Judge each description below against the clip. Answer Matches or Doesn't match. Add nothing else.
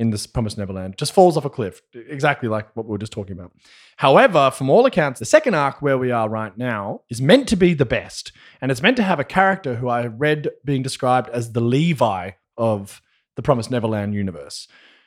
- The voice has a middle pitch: Doesn't match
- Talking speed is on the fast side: Matches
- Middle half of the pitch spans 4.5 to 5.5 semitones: Matches